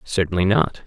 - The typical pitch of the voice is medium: No, very low, 90 Hz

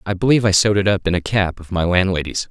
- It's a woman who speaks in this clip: No, male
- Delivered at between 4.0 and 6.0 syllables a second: No, 7.1 syllables/s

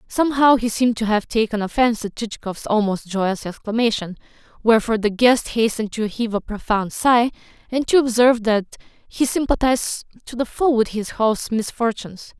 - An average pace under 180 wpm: Yes, average, 165 wpm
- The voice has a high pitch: Yes, high, 225 Hz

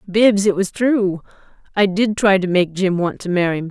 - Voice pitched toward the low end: No, high, 190 Hz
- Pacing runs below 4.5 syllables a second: No, 4.9 syllables/s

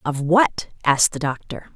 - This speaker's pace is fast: No, average, 170 wpm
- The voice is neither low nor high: Yes, medium, 155 Hz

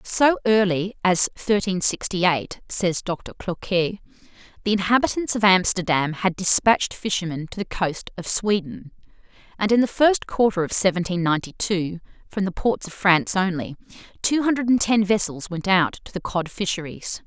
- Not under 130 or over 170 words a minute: Yes, average, 160 wpm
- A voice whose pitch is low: No, high, 190 Hz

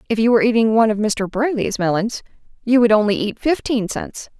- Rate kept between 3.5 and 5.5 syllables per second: No, 5.9 syllables/s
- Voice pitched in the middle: No, high, 225 Hz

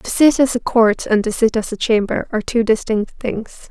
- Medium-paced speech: No, fast, 245 wpm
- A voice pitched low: No, high, 225 Hz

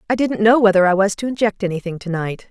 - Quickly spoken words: Yes, fast, 265 wpm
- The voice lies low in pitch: No, high, 200 Hz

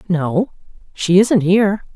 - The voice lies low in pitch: No, high, 190 Hz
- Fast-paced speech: No, slow, 125 wpm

